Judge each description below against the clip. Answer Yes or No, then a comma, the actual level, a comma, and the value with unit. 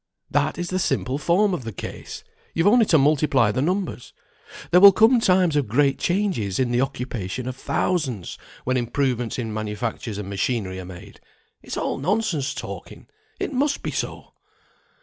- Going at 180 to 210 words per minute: No, average, 170 wpm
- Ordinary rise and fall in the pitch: No, wide, 8.0 semitones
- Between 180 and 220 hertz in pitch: No, low, 135 Hz